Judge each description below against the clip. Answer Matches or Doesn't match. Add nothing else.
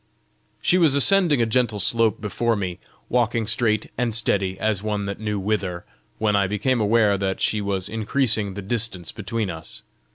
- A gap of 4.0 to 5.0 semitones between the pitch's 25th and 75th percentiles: Doesn't match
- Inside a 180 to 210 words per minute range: Doesn't match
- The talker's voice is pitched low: Matches